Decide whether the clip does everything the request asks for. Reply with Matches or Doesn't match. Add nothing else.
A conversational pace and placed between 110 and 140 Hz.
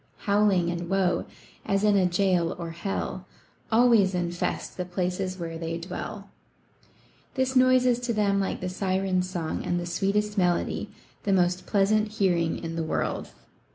Doesn't match